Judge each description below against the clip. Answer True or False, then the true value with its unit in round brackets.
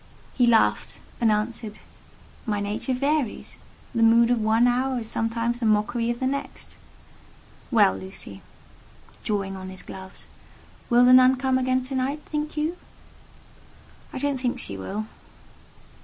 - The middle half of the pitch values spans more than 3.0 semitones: True (3.5 semitones)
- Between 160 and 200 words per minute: False (145 wpm)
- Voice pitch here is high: True (235 Hz)